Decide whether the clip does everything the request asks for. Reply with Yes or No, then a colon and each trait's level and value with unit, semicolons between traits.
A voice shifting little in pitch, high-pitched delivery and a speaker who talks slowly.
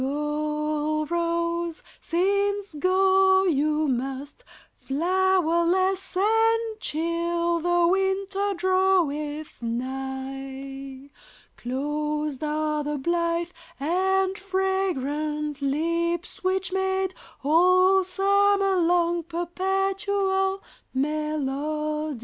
No: average, 4.2 semitones; very high, 340 Hz; slow, 75 wpm